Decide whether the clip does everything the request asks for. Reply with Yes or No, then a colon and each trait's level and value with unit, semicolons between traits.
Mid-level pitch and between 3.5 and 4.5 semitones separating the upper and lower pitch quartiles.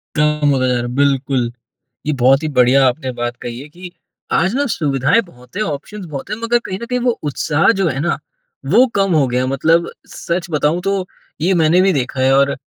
No: medium, 150 Hz; wide, 5.6 semitones